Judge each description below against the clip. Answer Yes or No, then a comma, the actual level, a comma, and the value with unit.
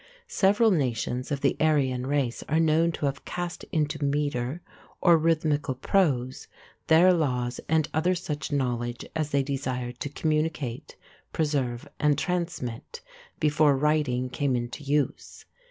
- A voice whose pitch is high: No, medium, 145 Hz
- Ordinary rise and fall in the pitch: Yes, average, 3.7 semitones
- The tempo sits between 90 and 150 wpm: Yes, slow, 135 wpm